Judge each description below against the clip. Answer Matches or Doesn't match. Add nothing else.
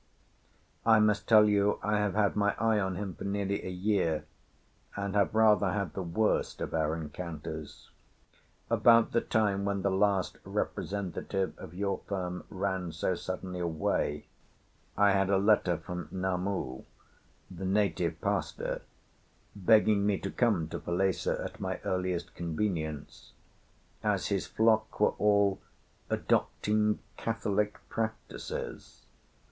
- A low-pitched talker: Matches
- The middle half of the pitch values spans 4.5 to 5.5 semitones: Doesn't match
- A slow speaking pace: Matches